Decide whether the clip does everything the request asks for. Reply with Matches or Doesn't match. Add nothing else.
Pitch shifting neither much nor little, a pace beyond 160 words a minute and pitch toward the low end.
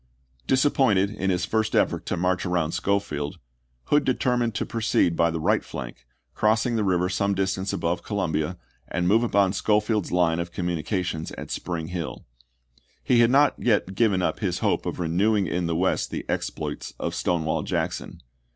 Matches